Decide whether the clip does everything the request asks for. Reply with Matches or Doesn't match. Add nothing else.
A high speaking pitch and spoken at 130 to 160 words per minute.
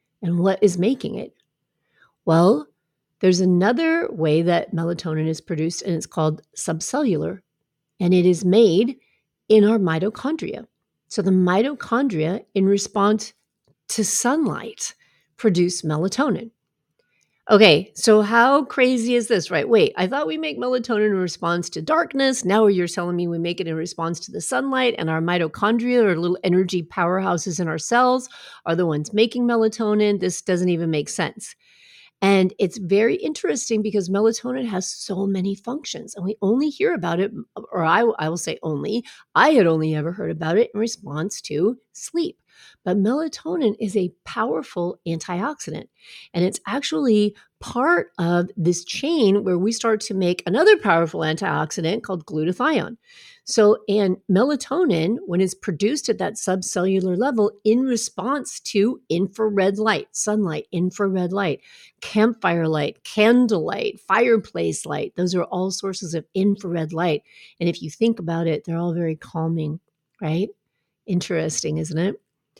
Matches